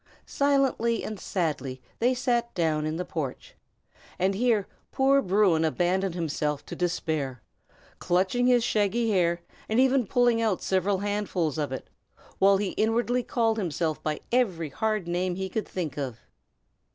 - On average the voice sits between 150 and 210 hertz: Yes, high, 190 Hz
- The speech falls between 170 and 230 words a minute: No, average, 150 wpm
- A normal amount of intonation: No, wide, 5.8 semitones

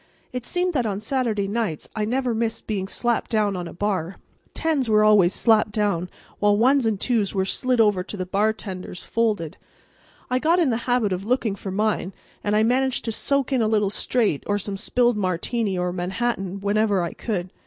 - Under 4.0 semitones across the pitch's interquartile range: Yes, average, 3.6 semitones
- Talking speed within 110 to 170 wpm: No, average, 195 wpm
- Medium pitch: No, high, 215 Hz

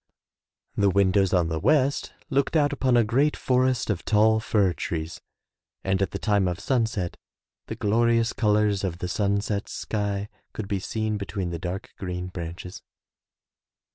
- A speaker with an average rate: Yes, average, 155 wpm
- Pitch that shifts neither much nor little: Yes, average, 3.7 semitones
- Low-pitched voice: Yes, low, 100 Hz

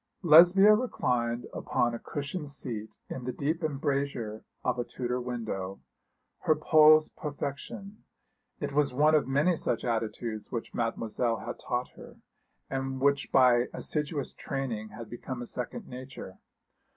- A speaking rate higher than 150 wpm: No, average, 140 wpm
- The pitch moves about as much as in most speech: Yes, average, 3.9 semitones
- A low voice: Yes, low, 130 Hz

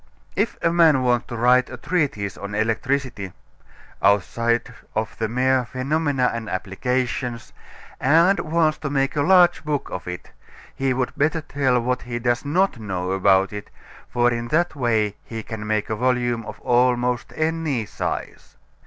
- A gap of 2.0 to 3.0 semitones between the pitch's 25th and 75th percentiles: No, average, 4.3 semitones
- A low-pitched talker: Yes, low, 125 Hz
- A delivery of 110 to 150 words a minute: No, average, 160 wpm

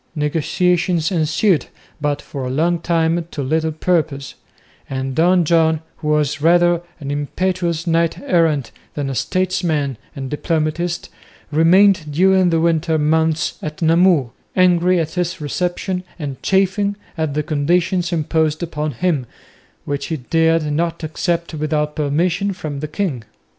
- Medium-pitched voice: Yes, medium, 160 Hz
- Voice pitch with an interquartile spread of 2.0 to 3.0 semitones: Yes, average, 2.7 semitones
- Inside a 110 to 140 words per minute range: Yes, slow, 135 wpm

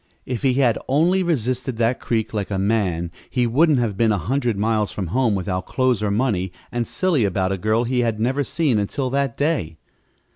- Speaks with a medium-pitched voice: No, low, 115 Hz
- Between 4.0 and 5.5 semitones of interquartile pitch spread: Yes, average, 4.4 semitones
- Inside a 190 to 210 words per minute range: Yes, fast, 205 wpm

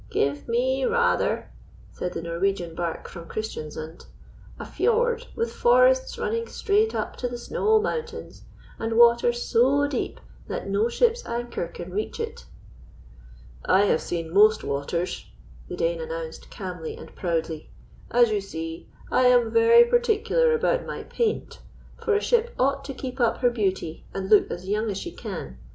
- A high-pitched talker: Yes, high, 240 Hz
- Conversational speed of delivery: Yes, average, 160 wpm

